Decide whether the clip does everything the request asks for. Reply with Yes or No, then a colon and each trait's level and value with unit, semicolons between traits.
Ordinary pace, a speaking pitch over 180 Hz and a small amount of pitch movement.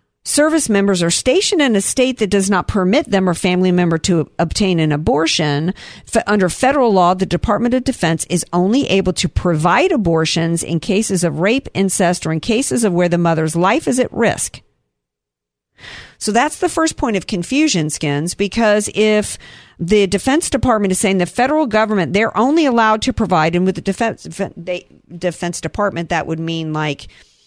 No: average, 175 wpm; high, 190 Hz; average, 4.8 semitones